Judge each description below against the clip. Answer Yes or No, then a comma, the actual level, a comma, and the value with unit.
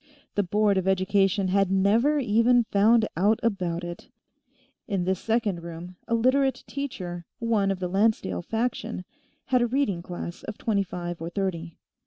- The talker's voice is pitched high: Yes, high, 200 Hz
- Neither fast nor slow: Yes, average, 160 wpm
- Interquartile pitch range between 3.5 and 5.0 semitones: Yes, average, 4.2 semitones